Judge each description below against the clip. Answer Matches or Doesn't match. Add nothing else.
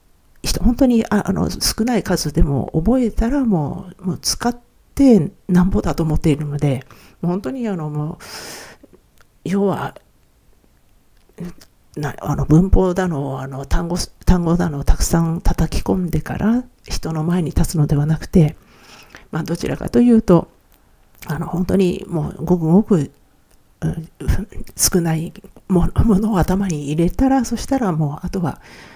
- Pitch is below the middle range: Doesn't match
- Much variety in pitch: Doesn't match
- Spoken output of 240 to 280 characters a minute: Matches